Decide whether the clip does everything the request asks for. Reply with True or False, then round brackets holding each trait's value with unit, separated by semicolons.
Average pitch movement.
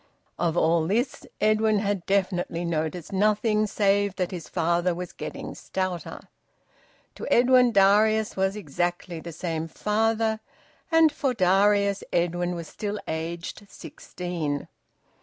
True (3.7 semitones)